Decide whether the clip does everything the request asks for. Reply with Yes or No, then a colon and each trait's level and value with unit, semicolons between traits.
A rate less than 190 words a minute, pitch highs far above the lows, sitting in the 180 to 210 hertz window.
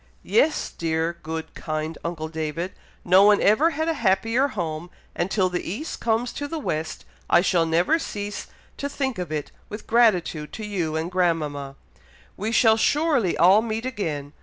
Yes: average, 170 wpm; wide, 5.9 semitones; medium, 185 Hz